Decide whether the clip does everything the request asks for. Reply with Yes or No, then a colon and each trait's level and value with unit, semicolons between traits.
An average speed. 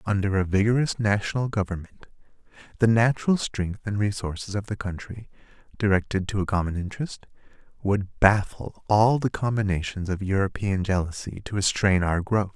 Yes: average, 145 wpm